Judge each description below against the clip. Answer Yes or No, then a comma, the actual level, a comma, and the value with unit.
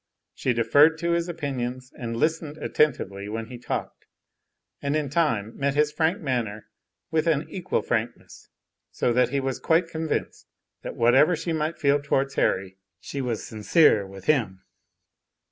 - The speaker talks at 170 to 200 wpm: No, average, 155 wpm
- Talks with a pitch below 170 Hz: Yes, medium, 140 Hz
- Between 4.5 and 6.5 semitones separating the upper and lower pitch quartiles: Yes, wide, 5.4 semitones